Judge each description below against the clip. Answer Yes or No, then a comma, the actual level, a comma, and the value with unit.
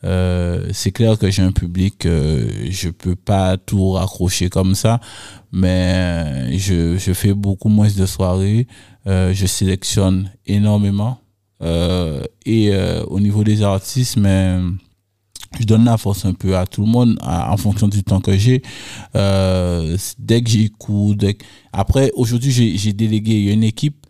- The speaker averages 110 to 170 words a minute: Yes, average, 165 wpm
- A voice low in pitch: Yes, low, 100 Hz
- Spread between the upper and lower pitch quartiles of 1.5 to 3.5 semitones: Yes, narrow, 2.6 semitones